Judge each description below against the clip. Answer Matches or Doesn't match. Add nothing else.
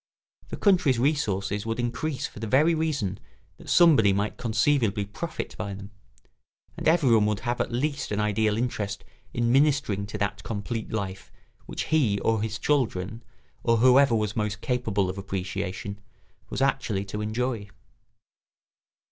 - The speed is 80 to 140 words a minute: Doesn't match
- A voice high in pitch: Doesn't match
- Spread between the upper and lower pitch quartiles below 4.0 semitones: Doesn't match